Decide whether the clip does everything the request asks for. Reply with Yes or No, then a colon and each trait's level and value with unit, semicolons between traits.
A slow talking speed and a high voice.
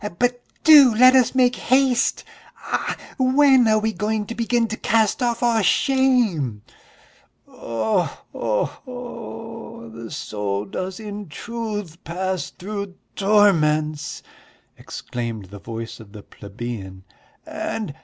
Yes: slow, 120 wpm; high, 210 Hz